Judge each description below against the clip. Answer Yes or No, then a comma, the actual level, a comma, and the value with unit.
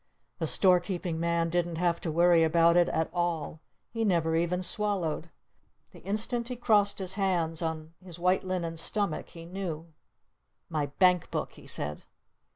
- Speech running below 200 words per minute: Yes, average, 165 wpm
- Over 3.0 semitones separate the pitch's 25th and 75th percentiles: No, narrow, 2.4 semitones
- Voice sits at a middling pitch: Yes, medium, 175 Hz